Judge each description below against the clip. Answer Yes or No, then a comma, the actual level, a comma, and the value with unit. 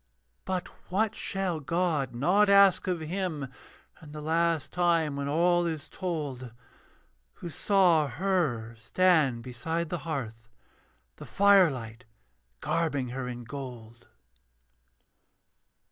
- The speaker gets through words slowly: Yes, slow, 110 wpm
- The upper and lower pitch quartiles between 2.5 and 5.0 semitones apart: No, wide, 5.5 semitones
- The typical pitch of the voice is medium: Yes, medium, 160 Hz